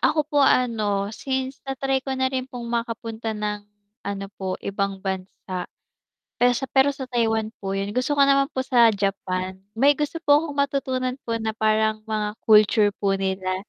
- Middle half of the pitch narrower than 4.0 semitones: No, average, 4.7 semitones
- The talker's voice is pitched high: Yes, high, 225 Hz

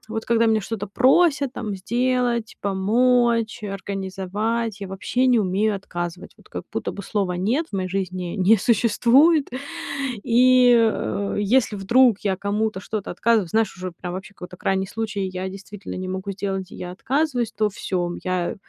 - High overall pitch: Yes, high, 205 Hz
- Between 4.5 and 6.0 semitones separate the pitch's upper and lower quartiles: No, average, 3.6 semitones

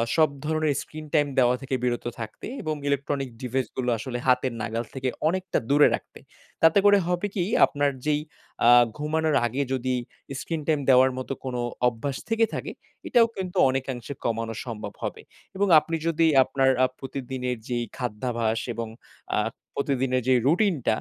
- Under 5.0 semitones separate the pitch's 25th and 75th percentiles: Yes, average, 3.9 semitones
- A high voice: No, low, 135 Hz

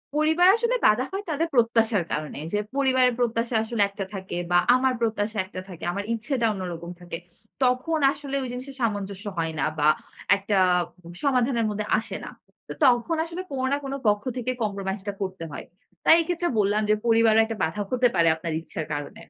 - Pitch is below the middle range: No, high, 225 Hz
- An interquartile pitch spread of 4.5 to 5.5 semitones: Yes, average, 4.8 semitones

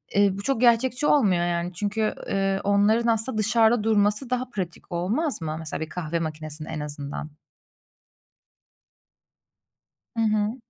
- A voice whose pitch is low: No, high, 205 Hz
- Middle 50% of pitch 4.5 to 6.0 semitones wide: Yes, average, 4.9 semitones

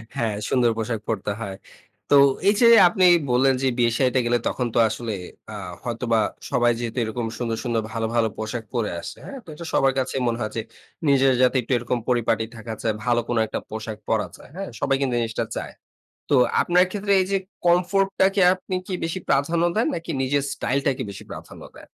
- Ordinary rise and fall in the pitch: No, wide, 5.8 semitones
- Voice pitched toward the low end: Yes, low, 125 Hz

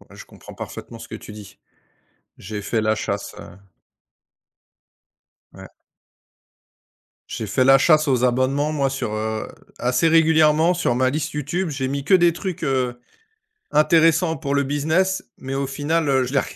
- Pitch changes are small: No, average, 3.7 semitones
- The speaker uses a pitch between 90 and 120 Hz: No, medium, 140 Hz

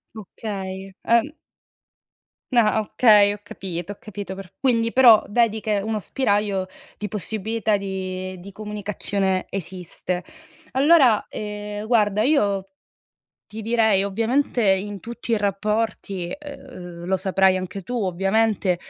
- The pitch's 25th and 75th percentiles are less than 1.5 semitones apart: No, narrow, 2.5 semitones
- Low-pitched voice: No, high, 205 Hz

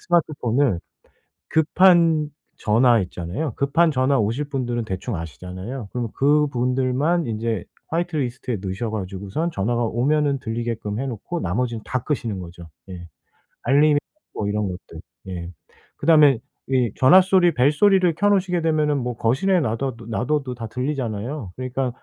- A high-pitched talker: No, low, 125 Hz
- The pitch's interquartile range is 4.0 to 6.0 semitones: Yes, wide, 5.4 semitones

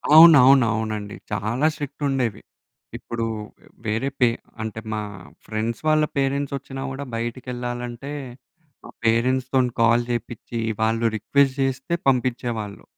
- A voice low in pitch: Yes, low, 120 Hz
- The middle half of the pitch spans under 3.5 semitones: Yes, average, 2.9 semitones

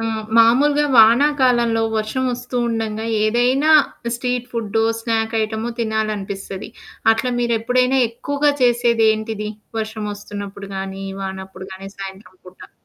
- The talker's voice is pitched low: No, high, 225 Hz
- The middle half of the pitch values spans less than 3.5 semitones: Yes, average, 3.0 semitones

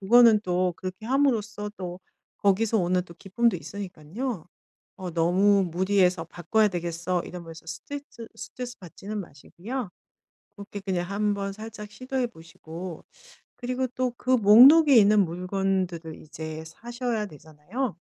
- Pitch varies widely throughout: No, average, 4.5 semitones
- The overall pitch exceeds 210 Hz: No, high, 195 Hz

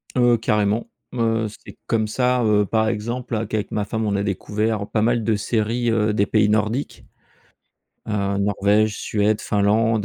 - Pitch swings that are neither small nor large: No, narrow, 1.6 semitones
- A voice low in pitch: Yes, low, 110 Hz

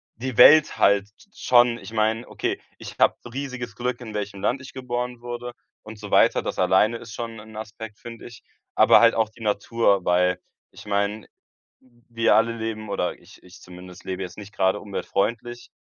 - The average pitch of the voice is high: No, low, 110 Hz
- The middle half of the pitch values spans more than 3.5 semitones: No, average, 2.8 semitones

